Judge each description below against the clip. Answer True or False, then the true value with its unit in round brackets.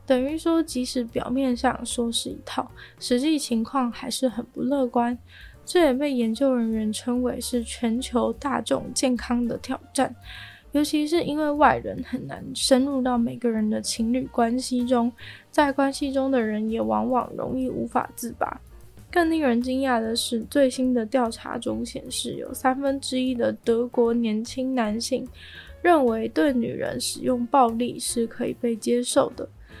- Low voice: False (250 Hz)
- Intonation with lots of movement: False (2.1 semitones)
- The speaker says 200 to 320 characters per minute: True (240 characters per minute)